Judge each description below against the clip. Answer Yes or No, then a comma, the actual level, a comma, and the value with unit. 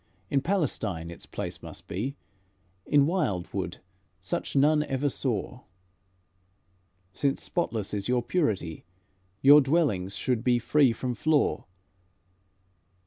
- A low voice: Yes, low, 130 Hz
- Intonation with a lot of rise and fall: Yes, wide, 6.1 semitones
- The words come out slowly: Yes, slow, 110 wpm